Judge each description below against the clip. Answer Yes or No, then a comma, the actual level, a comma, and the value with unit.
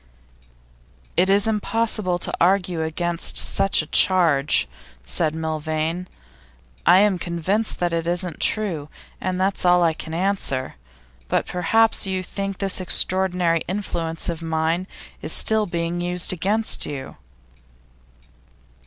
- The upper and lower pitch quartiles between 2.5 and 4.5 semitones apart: Yes, average, 2.9 semitones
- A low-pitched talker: No, medium, 180 Hz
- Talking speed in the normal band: No, slow, 120 wpm